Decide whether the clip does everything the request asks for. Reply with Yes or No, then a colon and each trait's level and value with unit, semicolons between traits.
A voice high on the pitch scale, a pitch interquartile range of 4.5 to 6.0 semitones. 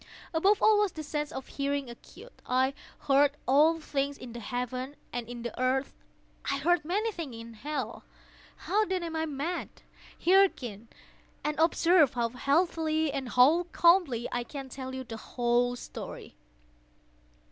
Yes: very high, 280 Hz; average, 4.8 semitones